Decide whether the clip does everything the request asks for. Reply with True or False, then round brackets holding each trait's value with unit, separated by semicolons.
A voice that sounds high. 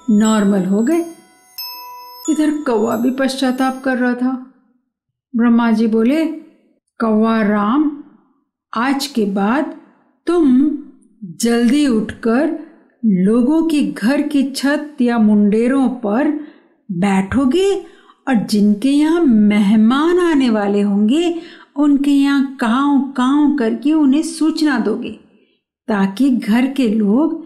True (265 Hz)